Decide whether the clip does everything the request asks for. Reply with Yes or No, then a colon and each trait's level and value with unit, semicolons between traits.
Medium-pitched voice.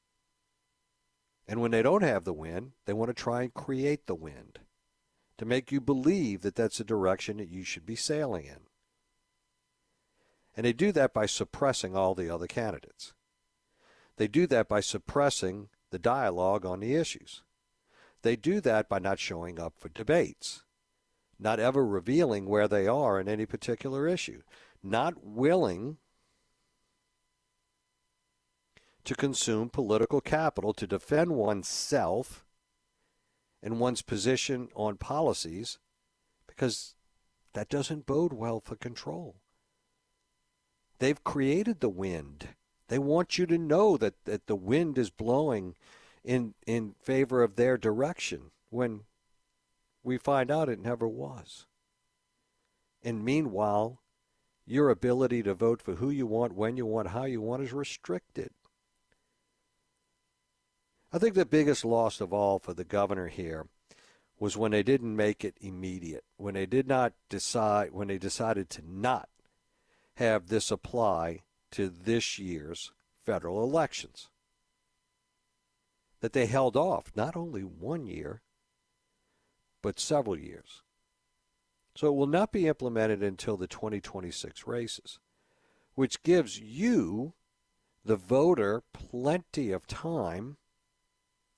No: low, 115 Hz